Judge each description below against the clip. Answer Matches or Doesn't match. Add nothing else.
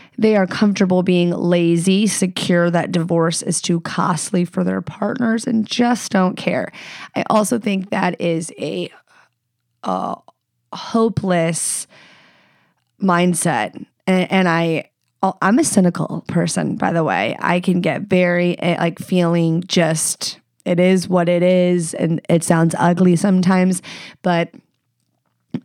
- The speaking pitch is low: Doesn't match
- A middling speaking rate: Doesn't match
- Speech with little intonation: Matches